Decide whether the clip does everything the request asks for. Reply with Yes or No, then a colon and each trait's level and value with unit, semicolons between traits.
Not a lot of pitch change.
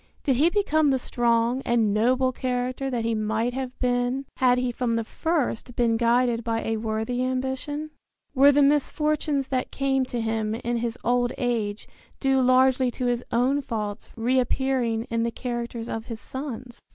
Yes: narrow, 2.3 semitones